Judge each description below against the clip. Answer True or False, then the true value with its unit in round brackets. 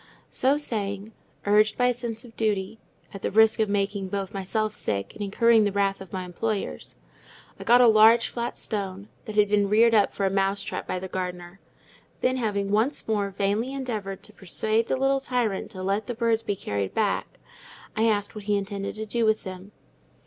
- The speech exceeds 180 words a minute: True (190 wpm)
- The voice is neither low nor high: False (210 Hz)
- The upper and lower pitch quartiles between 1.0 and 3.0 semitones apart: True (2.4 semitones)